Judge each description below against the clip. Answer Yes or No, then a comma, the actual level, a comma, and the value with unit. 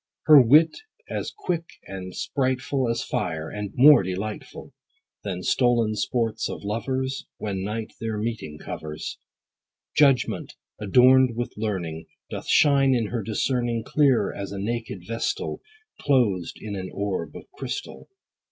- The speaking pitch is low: Yes, low, 115 Hz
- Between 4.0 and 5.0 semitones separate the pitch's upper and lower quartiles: Yes, average, 4.5 semitones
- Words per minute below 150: Yes, slow, 135 wpm